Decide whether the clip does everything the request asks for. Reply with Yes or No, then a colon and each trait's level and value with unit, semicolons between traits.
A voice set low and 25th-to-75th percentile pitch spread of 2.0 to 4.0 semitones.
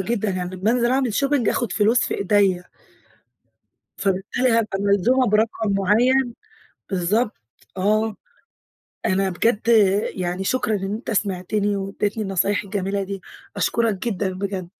No: high, 205 Hz; average, 3.0 semitones